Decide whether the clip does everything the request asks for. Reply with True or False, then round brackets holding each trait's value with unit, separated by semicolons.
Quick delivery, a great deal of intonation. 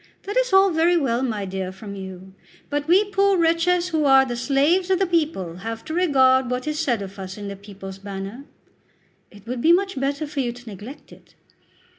True (210 wpm; 8.7 semitones)